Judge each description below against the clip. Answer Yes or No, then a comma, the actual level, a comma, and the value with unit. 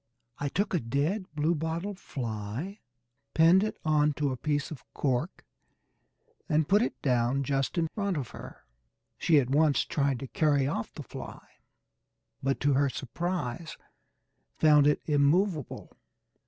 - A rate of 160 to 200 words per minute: No, average, 140 wpm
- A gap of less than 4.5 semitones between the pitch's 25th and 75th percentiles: Yes, average, 3.6 semitones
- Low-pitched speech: No, medium, 150 Hz